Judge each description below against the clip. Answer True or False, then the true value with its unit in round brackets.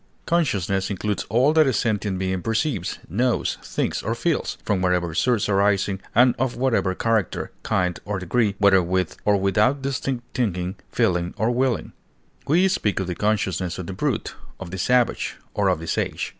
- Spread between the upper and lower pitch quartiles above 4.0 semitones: True (4.7 semitones)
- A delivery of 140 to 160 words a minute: False (170 wpm)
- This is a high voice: False (105 Hz)